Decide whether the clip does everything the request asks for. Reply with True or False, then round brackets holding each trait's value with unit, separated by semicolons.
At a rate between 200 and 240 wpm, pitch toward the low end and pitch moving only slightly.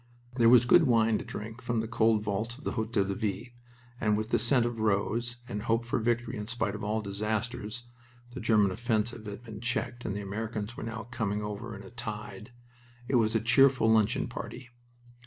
True (205 wpm; 110 Hz; 2.1 semitones)